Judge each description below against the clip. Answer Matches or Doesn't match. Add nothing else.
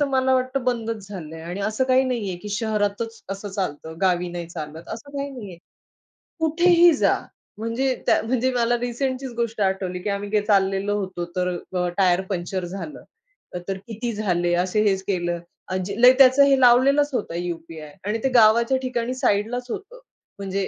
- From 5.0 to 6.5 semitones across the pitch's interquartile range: Matches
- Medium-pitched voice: Doesn't match